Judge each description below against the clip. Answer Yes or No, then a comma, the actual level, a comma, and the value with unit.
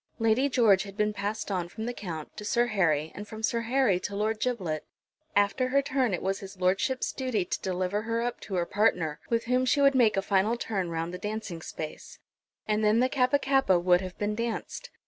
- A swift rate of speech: Yes, fast, 220 wpm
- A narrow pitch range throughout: No, average, 4.3 semitones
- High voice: Yes, high, 210 Hz